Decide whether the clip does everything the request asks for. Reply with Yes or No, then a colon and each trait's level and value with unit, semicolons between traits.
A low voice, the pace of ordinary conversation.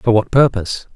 Yes: low, 110 Hz; average, 190 wpm